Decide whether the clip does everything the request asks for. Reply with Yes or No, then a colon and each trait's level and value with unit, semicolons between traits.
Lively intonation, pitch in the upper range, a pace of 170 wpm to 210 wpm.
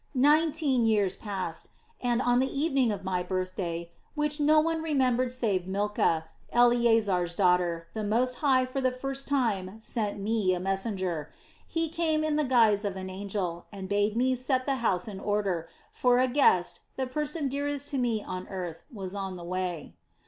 Yes: wide, 5.8 semitones; high, 220 Hz; average, 175 wpm